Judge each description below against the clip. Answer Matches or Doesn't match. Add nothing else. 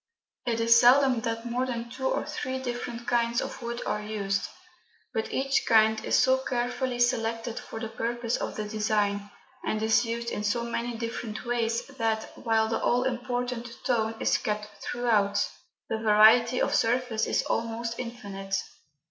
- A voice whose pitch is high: Matches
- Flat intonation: Matches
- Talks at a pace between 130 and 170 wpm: Matches